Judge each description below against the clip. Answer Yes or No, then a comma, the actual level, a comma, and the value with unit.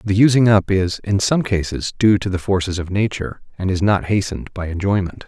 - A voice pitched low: Yes, low, 100 Hz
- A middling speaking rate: No, fast, 215 wpm